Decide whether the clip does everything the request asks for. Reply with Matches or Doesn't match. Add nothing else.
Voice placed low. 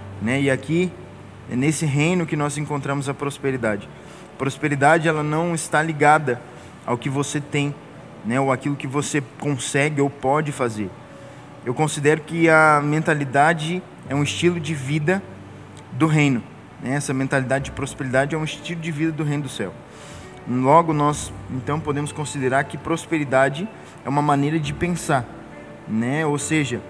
Doesn't match